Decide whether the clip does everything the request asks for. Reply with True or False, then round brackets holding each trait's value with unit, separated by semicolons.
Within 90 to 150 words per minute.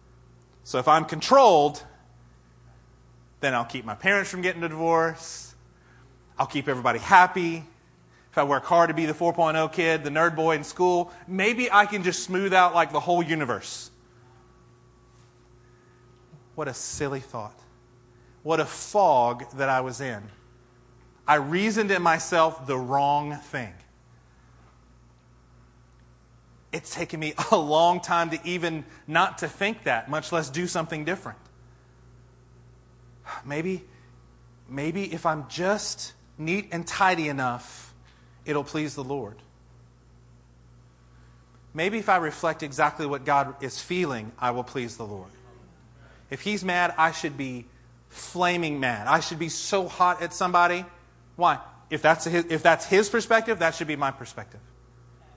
True (140 wpm)